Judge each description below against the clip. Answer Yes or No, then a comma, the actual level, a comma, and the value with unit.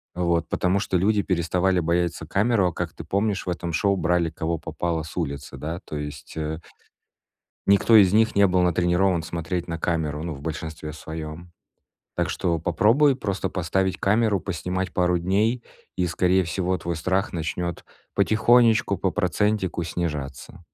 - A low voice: Yes, very low, 90 Hz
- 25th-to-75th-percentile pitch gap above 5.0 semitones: No, average, 3.0 semitones